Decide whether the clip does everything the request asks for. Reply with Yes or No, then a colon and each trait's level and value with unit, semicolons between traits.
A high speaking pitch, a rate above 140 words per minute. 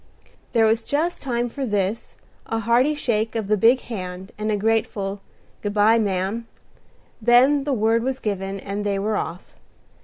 Yes: high, 220 Hz; average, 165 wpm